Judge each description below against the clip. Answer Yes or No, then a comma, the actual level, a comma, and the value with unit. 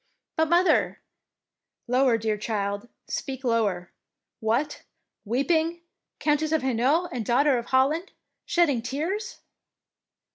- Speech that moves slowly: Yes, slow, 120 wpm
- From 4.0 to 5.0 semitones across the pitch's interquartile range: No, wide, 5.6 semitones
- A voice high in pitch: Yes, very high, 265 Hz